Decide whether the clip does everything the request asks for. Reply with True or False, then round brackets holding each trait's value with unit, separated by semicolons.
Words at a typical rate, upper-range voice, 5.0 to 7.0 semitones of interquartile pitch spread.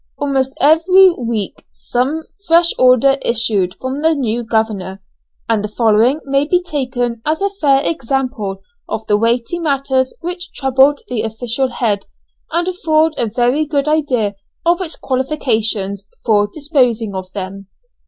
True (145 wpm; 260 Hz; 5.4 semitones)